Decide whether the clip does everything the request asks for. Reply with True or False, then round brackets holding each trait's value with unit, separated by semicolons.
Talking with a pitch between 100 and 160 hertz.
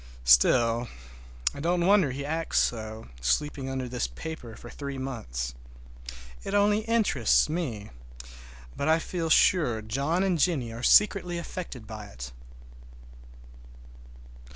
True (140 Hz)